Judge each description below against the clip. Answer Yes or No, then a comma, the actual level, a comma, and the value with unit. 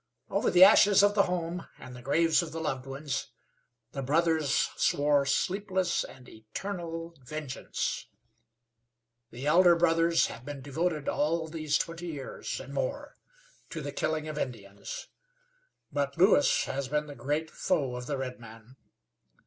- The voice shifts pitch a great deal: No, average, 3.8 semitones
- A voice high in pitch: No, medium, 155 Hz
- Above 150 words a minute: No, average, 145 wpm